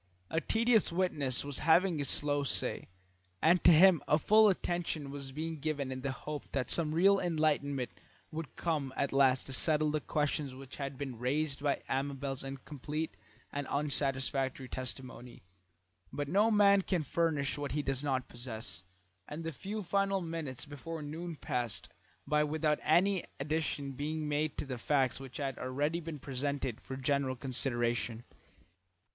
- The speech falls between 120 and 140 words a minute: No, average, 160 wpm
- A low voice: No, medium, 145 Hz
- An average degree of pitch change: Yes, average, 3.2 semitones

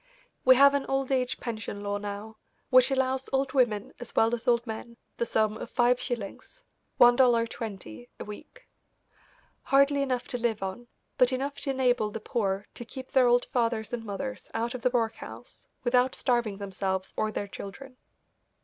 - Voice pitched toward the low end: No, high, 240 Hz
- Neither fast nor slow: Yes, average, 170 wpm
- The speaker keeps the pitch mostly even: No, average, 3.1 semitones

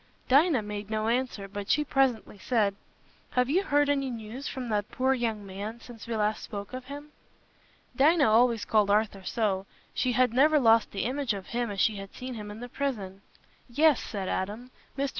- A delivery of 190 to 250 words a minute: Yes, average, 195 wpm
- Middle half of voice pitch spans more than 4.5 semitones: No, average, 4.1 semitones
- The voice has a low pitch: No, high, 230 Hz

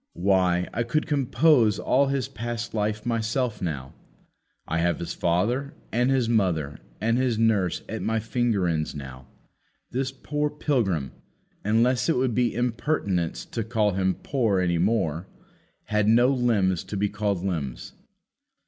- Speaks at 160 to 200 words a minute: No, average, 150 wpm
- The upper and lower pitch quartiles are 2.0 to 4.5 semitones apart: No, average, 5.2 semitones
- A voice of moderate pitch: No, low, 110 Hz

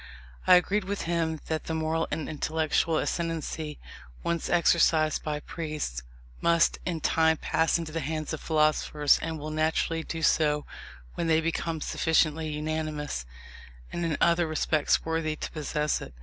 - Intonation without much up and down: Yes, narrow, 1.3 semitones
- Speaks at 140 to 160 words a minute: Yes, average, 150 wpm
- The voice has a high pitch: No, medium, 160 Hz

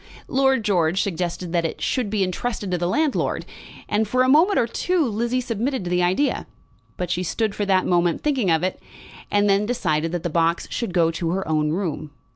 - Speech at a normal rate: No, fast, 210 wpm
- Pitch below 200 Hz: Yes, high, 190 Hz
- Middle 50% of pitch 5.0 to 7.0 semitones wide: Yes, wide, 5.5 semitones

